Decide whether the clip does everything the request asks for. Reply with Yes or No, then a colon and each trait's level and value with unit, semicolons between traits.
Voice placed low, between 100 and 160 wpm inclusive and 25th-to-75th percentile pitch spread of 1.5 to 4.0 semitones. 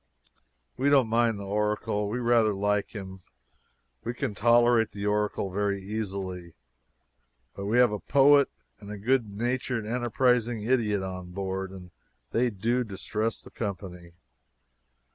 Yes: low, 105 Hz; average, 140 wpm; average, 3.3 semitones